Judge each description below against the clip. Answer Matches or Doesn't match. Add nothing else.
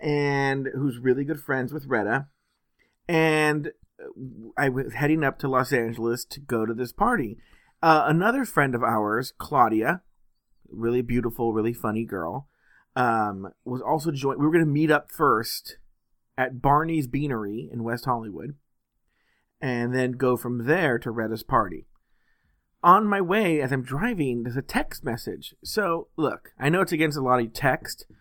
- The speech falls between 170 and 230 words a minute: Doesn't match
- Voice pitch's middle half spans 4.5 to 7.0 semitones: Doesn't match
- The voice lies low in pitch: Matches